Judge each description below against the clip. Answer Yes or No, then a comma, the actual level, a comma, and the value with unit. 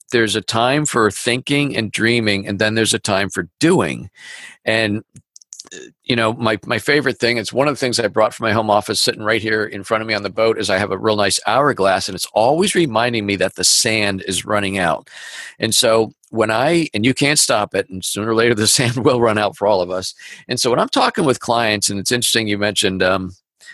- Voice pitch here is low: Yes, low, 110 Hz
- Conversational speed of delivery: No, fast, 240 wpm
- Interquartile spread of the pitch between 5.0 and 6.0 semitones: No, narrow, 2.6 semitones